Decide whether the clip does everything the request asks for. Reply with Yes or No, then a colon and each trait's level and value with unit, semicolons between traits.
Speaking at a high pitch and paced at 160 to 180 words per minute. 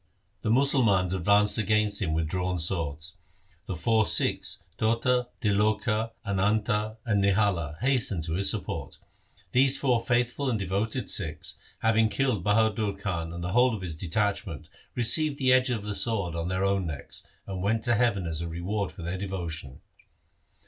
No: low, 100 Hz; average, 165 wpm